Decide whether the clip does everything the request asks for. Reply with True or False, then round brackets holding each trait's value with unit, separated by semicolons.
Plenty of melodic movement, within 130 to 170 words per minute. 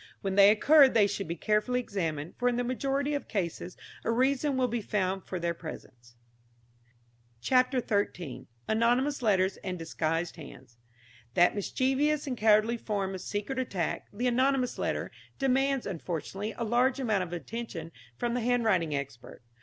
True (5.9 semitones; 155 wpm)